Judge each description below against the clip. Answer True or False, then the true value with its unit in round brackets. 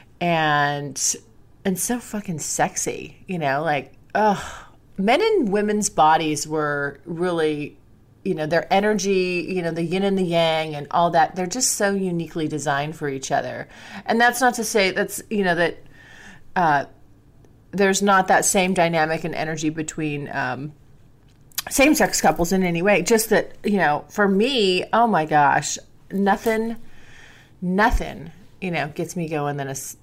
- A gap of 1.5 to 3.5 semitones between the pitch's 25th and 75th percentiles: False (5.3 semitones)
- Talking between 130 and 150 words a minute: False (160 wpm)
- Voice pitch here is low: False (170 Hz)